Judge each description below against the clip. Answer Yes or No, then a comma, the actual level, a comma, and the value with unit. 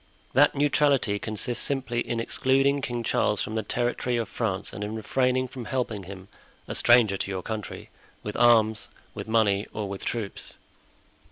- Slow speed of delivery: No, average, 155 wpm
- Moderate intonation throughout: Yes, average, 3.4 semitones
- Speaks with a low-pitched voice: Yes, low, 115 Hz